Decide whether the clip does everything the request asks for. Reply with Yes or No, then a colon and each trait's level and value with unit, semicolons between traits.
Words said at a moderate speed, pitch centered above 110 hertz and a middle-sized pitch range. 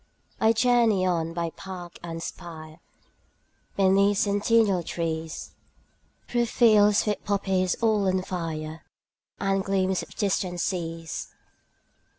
No: slow, 115 wpm; high, 190 Hz; average, 3.4 semitones